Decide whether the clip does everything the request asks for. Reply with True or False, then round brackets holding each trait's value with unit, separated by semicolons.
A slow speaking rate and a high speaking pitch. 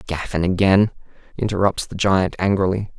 False (120 wpm; 95 Hz)